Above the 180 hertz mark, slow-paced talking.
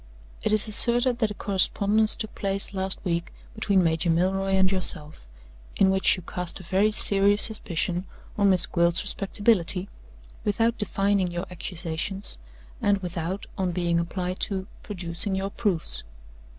No: high, 190 Hz; average, 145 wpm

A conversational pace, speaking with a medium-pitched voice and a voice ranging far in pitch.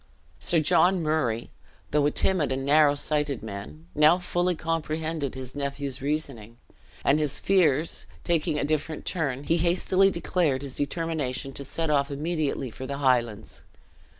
No: average, 150 wpm; medium, 150 Hz; average, 3.3 semitones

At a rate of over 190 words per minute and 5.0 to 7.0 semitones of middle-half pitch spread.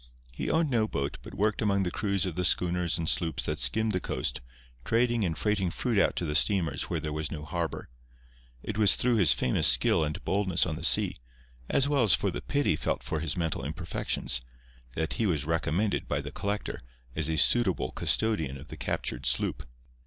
Yes: fast, 205 wpm; average, 5.3 semitones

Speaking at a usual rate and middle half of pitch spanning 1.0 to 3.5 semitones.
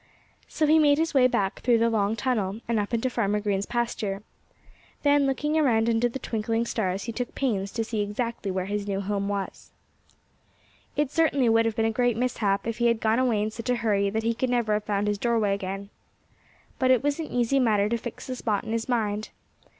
No: fast, 220 wpm; average, 3.1 semitones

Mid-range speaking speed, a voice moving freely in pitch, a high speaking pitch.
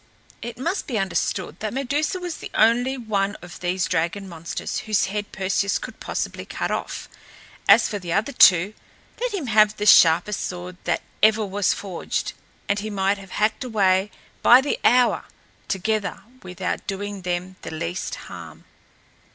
No: average, 160 wpm; average, 3.1 semitones; high, 205 Hz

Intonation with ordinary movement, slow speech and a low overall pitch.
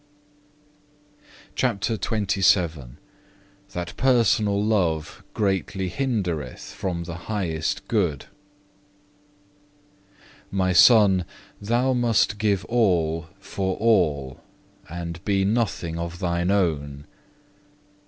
Yes: average, 3.9 semitones; slow, 85 wpm; very low, 95 Hz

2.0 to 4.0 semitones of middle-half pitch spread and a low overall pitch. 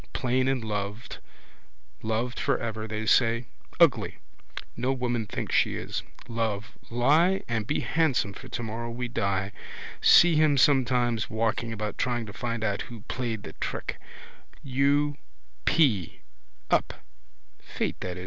Yes: average, 3.1 semitones; low, 120 Hz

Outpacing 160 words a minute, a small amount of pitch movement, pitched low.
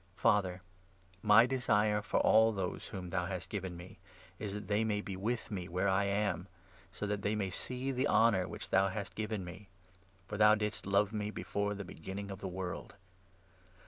Yes: average, 175 wpm; narrow, 2.0 semitones; low, 100 Hz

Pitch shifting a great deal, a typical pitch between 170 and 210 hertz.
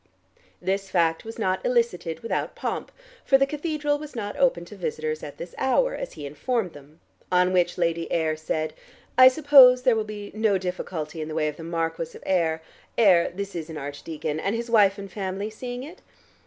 Yes: wide, 6.3 semitones; high, 190 Hz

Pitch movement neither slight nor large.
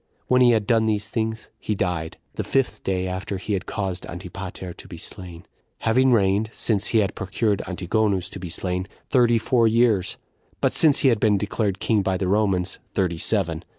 Yes: average, 3.3 semitones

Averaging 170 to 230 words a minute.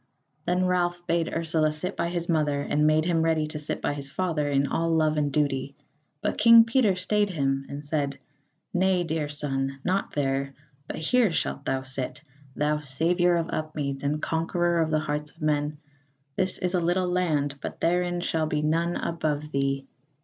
Yes: average, 185 wpm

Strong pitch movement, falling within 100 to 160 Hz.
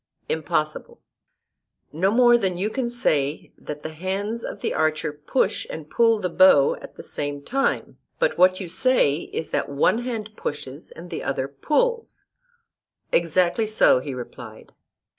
No: wide, 7.9 semitones; medium, 185 Hz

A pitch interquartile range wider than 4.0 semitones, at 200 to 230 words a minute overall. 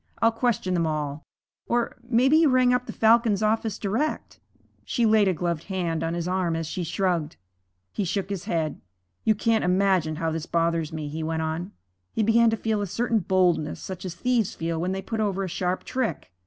Yes: average, 5.1 semitones; fast, 205 wpm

